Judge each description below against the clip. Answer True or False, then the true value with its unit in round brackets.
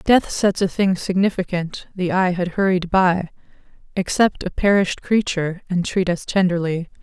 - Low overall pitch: False (185 Hz)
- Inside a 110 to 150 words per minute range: True (145 wpm)